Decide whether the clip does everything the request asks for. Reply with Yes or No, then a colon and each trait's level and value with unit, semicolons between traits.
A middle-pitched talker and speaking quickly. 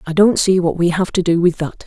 Yes: medium, 175 Hz; fast, 320 wpm